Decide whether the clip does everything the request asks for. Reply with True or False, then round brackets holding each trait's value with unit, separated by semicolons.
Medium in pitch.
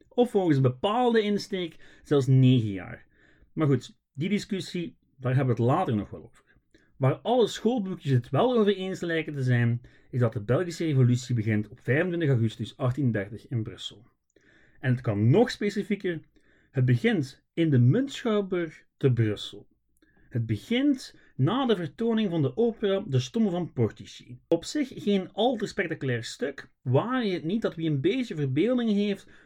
True (155 Hz)